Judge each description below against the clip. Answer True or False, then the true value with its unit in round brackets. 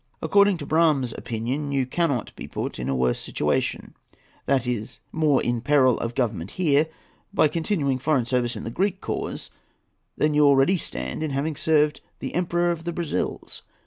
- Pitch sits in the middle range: True (145 Hz)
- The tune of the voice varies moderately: True (4.6 semitones)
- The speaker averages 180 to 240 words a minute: False (170 wpm)